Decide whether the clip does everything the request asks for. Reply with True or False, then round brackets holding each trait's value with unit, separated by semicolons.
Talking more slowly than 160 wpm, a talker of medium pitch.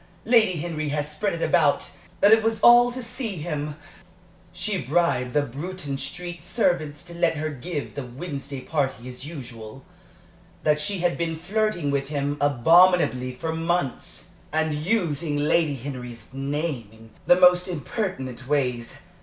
True (150 wpm; 155 Hz)